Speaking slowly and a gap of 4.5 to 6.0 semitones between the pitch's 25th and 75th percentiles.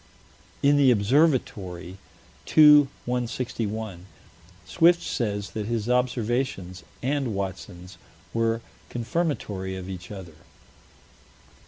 Yes: slow, 85 wpm; average, 5.2 semitones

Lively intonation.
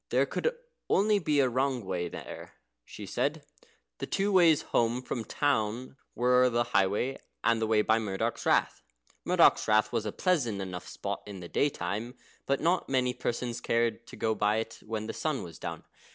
No: average, 4.0 semitones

